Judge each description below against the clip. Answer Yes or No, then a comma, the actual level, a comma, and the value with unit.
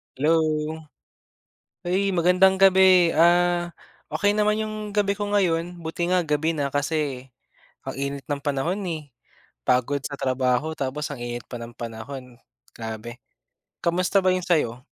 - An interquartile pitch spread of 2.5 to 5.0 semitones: No, wide, 5.6 semitones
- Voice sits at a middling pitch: Yes, medium, 160 Hz